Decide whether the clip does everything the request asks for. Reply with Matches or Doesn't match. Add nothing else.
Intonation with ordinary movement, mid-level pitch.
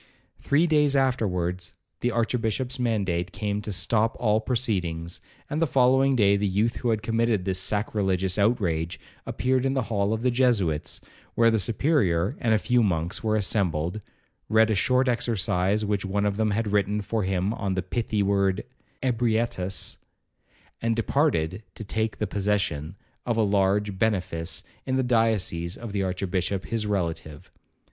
Doesn't match